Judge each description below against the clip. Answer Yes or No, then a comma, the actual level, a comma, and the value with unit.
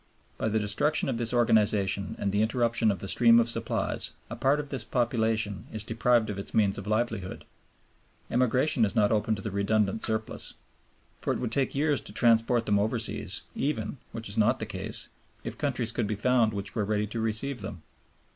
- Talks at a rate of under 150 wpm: No, average, 195 wpm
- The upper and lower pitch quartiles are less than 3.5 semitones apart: Yes, narrow, 2.4 semitones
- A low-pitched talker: Yes, low, 110 Hz